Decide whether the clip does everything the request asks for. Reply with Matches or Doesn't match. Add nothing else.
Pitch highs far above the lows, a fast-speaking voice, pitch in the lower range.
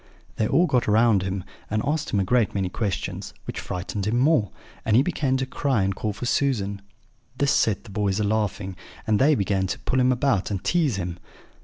Doesn't match